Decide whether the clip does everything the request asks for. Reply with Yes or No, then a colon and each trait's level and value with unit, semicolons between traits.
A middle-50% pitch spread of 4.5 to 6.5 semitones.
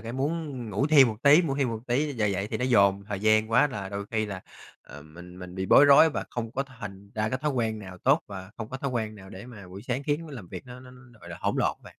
Yes: average, 5.2 semitones